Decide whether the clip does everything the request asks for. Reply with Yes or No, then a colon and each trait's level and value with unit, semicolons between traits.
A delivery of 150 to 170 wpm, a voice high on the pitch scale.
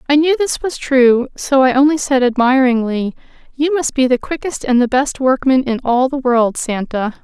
No: average, 200 wpm; very high, 260 Hz